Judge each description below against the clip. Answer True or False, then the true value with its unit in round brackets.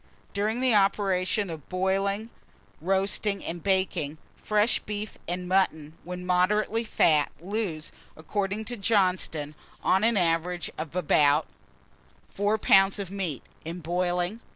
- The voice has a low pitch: False (185 Hz)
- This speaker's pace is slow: True (105 wpm)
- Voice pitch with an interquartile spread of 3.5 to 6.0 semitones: False (3.1 semitones)